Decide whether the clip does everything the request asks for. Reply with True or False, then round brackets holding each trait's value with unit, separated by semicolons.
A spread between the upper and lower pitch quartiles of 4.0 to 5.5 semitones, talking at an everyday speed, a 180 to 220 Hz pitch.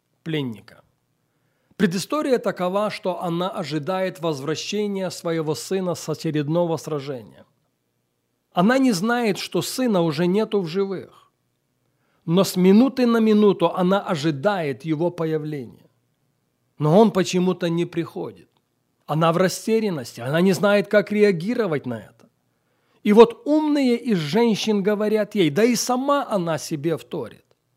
True (4.9 semitones; 125 wpm; 185 Hz)